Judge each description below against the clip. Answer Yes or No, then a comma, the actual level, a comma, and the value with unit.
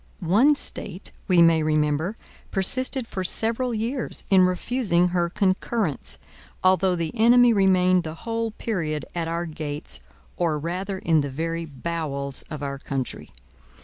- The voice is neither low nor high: Yes, medium, 180 Hz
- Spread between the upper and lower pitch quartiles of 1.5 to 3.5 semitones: No, average, 5.3 semitones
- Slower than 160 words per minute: Yes, average, 140 wpm